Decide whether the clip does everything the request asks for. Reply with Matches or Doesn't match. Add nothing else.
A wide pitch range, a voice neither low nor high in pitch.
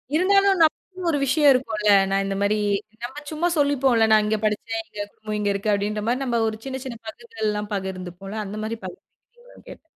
Doesn't match